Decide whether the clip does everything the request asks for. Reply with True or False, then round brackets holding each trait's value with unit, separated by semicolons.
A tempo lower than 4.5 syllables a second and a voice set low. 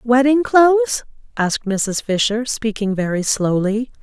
False (4.2 syllables/s; 235 Hz)